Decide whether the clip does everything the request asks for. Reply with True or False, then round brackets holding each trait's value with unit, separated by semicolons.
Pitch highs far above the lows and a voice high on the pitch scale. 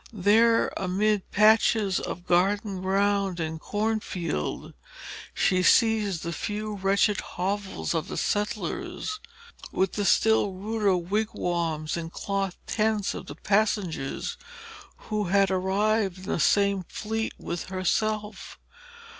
False (2.5 semitones; 200 Hz)